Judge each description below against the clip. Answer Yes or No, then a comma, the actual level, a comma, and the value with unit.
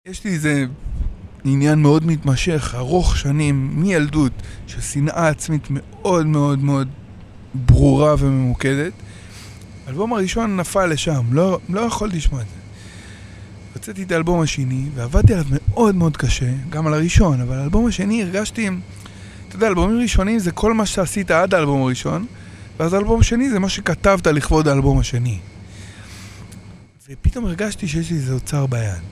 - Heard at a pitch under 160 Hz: Yes, medium, 140 Hz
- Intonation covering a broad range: Yes, wide, 8.2 semitones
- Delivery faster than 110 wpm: Yes, average, 145 wpm